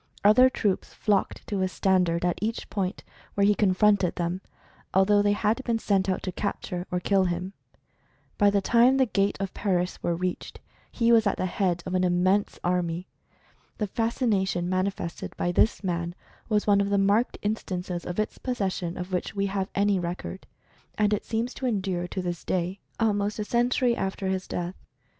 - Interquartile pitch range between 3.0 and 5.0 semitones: No, narrow, 2.6 semitones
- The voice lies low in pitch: No, high, 195 Hz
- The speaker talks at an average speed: Yes, average, 190 wpm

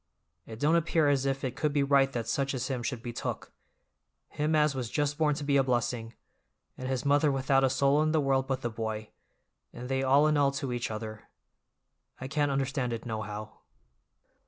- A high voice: No, low, 135 Hz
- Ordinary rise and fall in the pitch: Yes, average, 3.0 semitones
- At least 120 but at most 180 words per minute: No, fast, 205 wpm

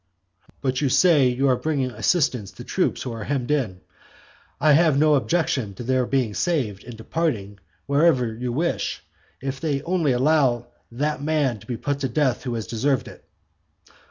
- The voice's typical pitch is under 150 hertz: Yes, low, 135 Hz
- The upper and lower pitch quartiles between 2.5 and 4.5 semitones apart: Yes, average, 3.8 semitones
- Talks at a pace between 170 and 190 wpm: Yes, average, 175 wpm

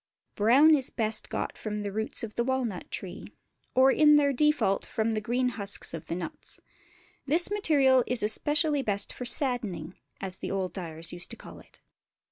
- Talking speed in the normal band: Yes, average, 180 wpm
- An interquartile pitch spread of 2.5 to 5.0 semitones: No, wide, 5.4 semitones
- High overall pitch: Yes, high, 230 Hz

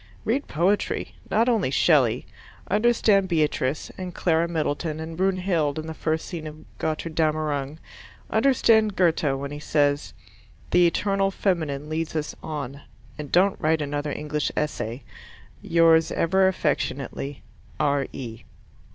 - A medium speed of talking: No, slow, 125 wpm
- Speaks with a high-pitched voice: No, medium, 160 Hz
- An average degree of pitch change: Yes, average, 4.0 semitones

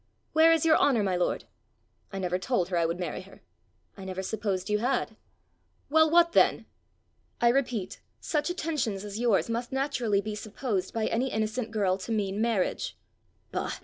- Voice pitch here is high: Yes, high, 220 Hz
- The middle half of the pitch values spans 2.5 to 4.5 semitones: No, average, 5.2 semitones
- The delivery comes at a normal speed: Yes, average, 175 wpm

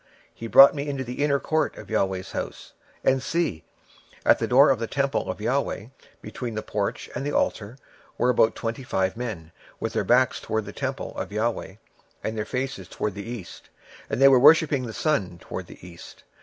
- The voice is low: Yes, low, 120 Hz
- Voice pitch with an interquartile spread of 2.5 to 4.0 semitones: No, average, 4.5 semitones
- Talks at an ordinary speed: No, fast, 215 wpm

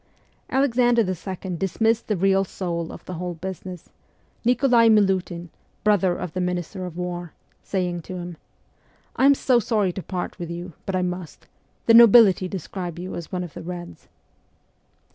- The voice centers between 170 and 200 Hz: Yes, medium, 185 Hz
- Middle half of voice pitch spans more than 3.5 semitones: No, average, 3.1 semitones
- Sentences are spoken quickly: No, average, 160 wpm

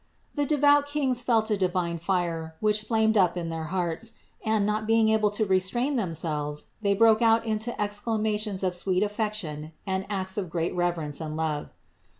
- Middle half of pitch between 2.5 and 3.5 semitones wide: No, average, 4.2 semitones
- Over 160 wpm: Yes, average, 170 wpm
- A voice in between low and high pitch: No, high, 205 Hz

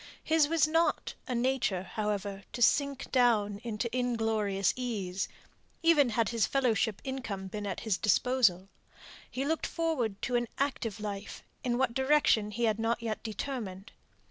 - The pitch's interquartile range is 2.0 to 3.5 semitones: No, average, 4.2 semitones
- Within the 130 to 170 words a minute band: Yes, average, 150 wpm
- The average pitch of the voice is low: No, high, 230 Hz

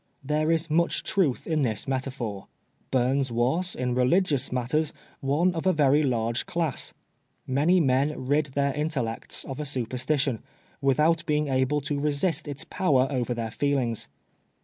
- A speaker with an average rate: Yes, average, 150 wpm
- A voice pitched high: No, medium, 140 Hz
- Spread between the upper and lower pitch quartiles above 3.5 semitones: No, average, 3.2 semitones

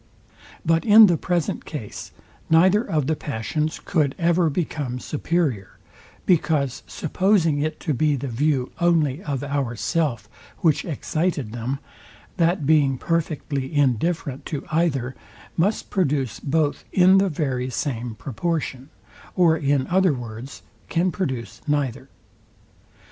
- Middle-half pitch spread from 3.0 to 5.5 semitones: Yes, average, 4.2 semitones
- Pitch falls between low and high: Yes, medium, 150 Hz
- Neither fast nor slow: No, slow, 120 wpm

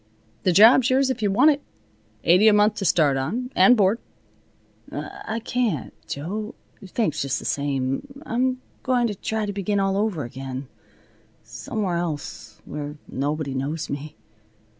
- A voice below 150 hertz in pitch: No, high, 195 Hz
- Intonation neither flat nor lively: No, wide, 7.7 semitones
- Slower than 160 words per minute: Yes, average, 150 wpm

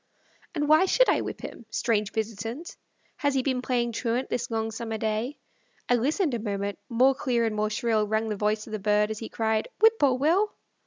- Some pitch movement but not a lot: Yes, average, 3.5 semitones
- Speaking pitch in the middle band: No, high, 230 Hz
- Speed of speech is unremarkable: No, fast, 210 wpm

